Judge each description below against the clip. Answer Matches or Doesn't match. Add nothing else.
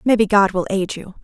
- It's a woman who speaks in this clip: Matches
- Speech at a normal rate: Doesn't match